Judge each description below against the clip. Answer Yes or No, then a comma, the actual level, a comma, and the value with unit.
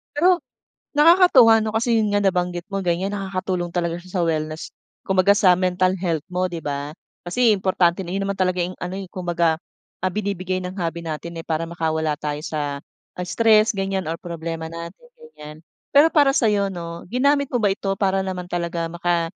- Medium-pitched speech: Yes, medium, 180 Hz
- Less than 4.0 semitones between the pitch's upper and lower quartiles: Yes, average, 3.1 semitones